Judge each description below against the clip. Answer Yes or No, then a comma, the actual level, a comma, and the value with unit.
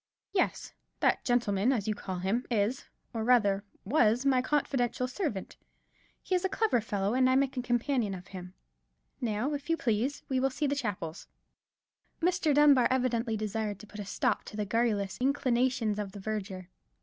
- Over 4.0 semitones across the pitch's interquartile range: Yes, average, 4.4 semitones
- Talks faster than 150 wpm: Yes, average, 175 wpm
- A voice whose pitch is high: Yes, high, 235 Hz